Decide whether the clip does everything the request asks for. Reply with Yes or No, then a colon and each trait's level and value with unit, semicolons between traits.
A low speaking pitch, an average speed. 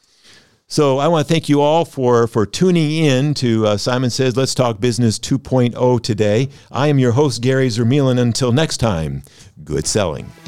Yes: low, 130 Hz; average, 180 wpm